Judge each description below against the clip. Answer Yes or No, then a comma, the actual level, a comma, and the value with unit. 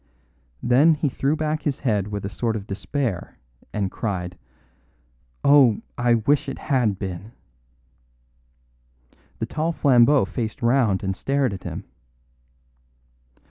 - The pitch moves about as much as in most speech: No, wide, 5.7 semitones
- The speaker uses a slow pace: Yes, slow, 125 wpm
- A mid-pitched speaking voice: No, low, 120 Hz